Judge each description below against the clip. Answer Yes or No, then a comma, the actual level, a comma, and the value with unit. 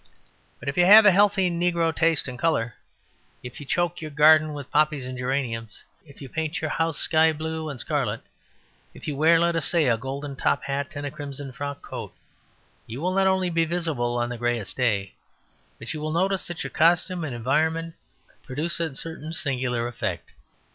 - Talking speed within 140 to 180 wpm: No, average, 195 wpm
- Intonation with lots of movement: No, average, 4.1 semitones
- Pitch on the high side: No, medium, 150 Hz